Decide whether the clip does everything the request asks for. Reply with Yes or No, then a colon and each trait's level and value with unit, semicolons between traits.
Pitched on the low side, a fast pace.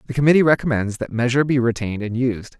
Yes: low, 125 Hz; fast, 210 wpm